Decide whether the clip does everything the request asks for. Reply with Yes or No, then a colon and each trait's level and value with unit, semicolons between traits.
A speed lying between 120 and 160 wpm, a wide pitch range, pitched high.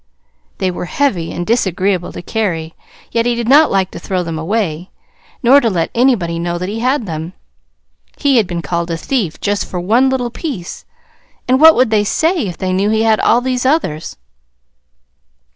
No: average, 190 wpm; wide, 6.0 semitones; high, 205 Hz